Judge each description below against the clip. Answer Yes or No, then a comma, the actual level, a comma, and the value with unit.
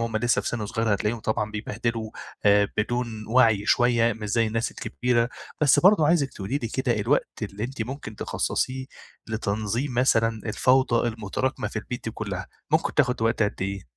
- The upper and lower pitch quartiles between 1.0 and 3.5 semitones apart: Yes, average, 2.7 semitones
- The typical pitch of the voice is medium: No, low, 115 Hz